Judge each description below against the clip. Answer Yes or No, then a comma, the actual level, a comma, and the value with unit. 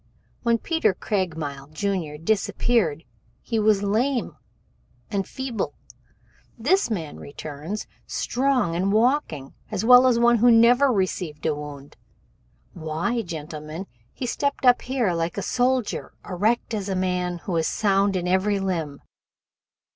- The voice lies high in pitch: Yes, high, 195 Hz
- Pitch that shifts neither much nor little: No, wide, 6.3 semitones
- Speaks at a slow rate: Yes, slow, 130 wpm